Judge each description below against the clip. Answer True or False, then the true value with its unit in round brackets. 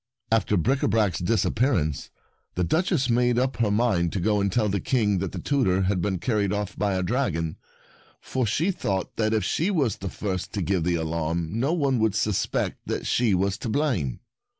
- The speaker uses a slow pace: False (195 wpm)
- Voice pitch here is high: False (105 Hz)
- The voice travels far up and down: False (5.0 semitones)